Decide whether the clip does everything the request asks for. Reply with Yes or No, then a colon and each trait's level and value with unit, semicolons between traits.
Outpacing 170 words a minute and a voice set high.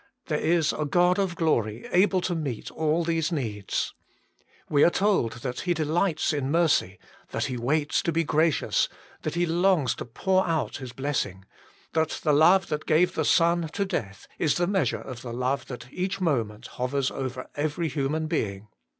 No: average, 180 wpm; medium, 155 Hz